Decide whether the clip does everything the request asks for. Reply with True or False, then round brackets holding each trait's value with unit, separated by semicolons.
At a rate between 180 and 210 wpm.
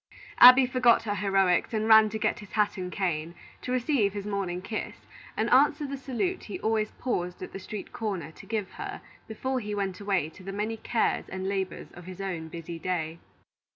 True (200 wpm)